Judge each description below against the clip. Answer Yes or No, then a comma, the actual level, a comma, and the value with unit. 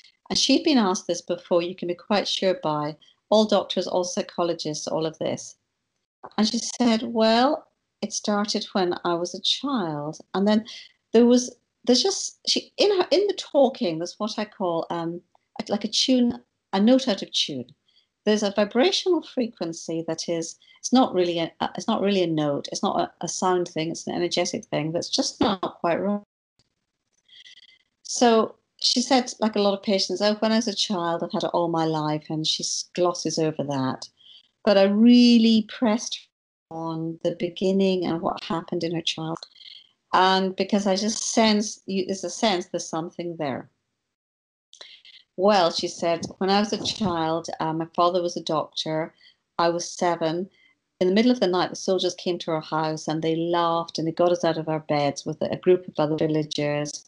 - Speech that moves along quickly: No, average, 190 wpm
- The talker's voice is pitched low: No, medium, 185 Hz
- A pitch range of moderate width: Yes, average, 4.7 semitones